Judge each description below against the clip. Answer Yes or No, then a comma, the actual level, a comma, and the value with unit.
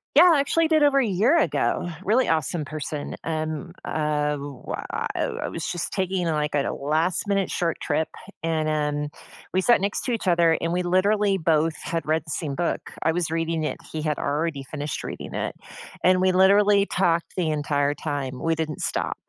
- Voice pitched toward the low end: No, medium, 165 Hz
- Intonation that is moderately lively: Yes, average, 3.6 semitones